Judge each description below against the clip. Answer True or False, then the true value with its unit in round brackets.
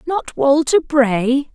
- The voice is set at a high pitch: True (280 Hz)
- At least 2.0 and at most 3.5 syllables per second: True (2.9 syllables/s)